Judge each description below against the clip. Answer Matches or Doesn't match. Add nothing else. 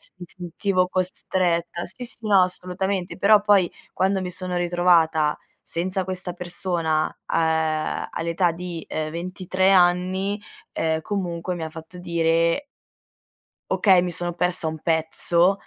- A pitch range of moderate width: Doesn't match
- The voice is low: Doesn't match